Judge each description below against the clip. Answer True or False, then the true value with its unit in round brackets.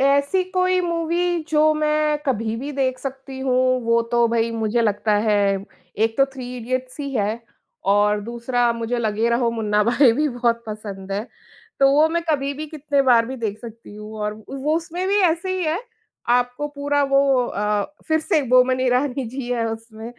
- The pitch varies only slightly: False (4.3 semitones)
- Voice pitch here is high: True (250 Hz)